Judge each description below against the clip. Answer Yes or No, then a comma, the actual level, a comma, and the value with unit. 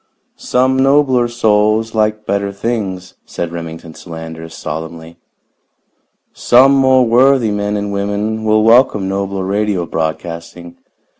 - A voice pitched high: No, low, 105 Hz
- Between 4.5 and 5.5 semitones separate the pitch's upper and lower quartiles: Yes, average, 5.1 semitones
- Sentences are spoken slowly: Yes, slow, 115 wpm